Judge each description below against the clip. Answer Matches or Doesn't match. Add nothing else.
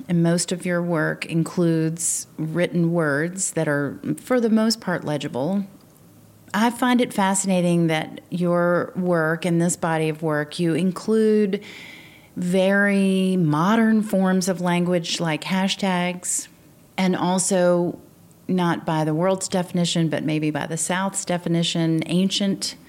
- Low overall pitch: Doesn't match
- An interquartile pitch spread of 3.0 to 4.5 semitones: Doesn't match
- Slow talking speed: Matches